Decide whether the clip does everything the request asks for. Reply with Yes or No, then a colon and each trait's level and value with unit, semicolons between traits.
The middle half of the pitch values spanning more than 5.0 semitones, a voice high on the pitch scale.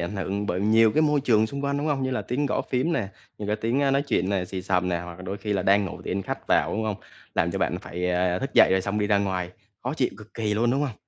No: wide, 5.4 semitones; low, 105 Hz